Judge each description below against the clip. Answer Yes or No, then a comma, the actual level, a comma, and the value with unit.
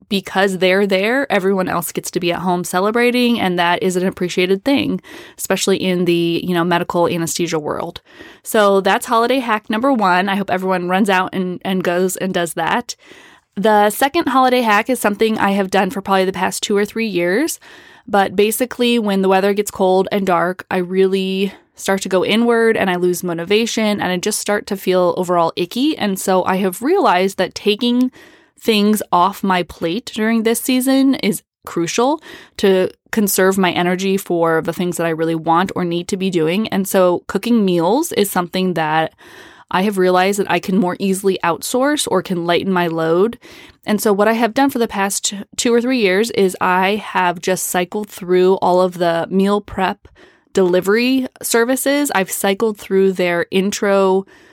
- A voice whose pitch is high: Yes, high, 195 Hz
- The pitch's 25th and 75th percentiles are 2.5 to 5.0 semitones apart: Yes, average, 3.4 semitones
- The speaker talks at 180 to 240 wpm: Yes, average, 185 wpm